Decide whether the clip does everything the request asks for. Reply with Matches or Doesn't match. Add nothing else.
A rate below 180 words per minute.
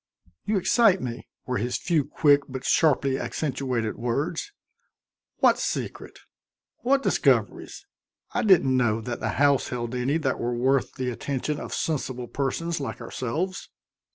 Matches